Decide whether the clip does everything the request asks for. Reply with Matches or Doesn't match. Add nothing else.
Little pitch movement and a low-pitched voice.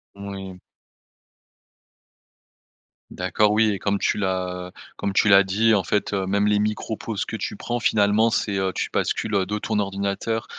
Matches